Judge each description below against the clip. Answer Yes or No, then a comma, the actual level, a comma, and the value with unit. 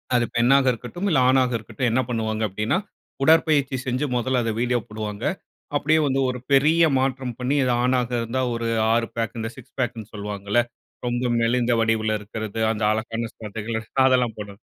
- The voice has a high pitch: No, low, 120 Hz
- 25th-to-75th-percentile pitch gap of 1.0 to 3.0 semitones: Yes, average, 2.7 semitones